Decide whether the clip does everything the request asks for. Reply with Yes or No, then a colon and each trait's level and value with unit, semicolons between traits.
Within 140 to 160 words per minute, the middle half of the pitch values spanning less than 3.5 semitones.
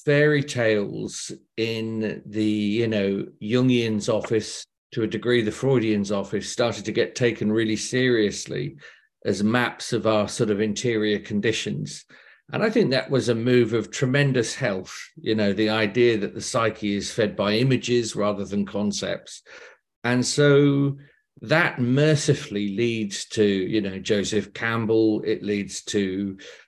Yes: average, 145 wpm; average, 3.0 semitones